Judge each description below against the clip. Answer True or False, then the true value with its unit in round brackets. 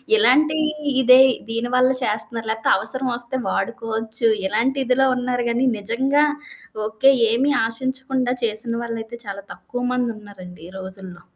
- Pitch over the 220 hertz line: True (235 Hz)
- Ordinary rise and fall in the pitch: True (3.1 semitones)